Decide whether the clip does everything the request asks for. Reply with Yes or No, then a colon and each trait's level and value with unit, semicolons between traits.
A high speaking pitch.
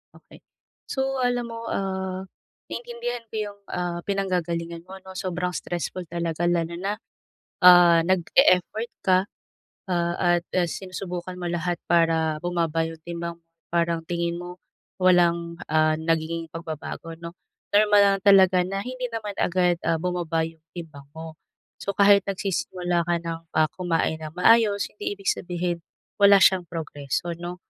No: medium, 175 Hz